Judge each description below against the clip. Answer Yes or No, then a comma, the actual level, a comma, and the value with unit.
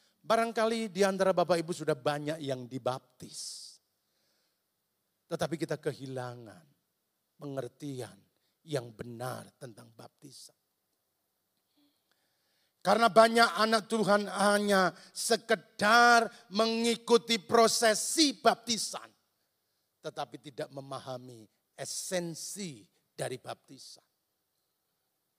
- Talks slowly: Yes, slow, 75 wpm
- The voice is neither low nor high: Yes, medium, 180 Hz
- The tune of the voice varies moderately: No, wide, 8.1 semitones